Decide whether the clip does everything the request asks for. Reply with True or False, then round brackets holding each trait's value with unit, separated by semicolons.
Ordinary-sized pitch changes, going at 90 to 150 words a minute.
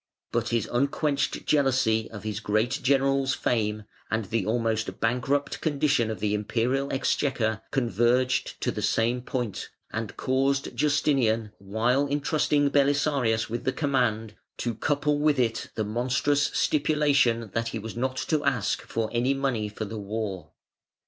True (3.8 semitones; 145 wpm)